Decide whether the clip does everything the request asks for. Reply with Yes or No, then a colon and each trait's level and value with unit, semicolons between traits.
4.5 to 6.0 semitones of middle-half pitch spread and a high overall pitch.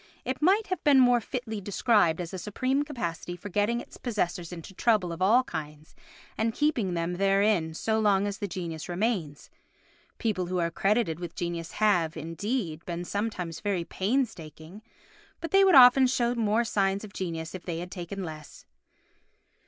Yes: average, 5.2 semitones; high, 195 Hz